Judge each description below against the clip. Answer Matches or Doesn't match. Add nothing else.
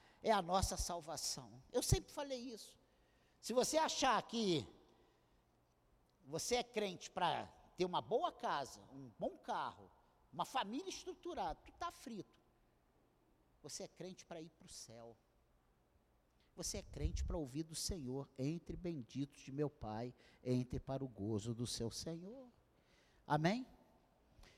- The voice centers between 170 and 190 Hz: Doesn't match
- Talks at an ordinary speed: Matches